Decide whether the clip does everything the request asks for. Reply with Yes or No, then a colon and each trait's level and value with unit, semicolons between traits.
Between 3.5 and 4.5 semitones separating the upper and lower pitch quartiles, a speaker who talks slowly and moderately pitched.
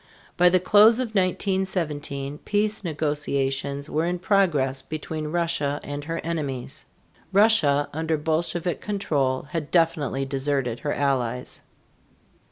Yes: average, 4.1 semitones; slow, 115 wpm; medium, 155 Hz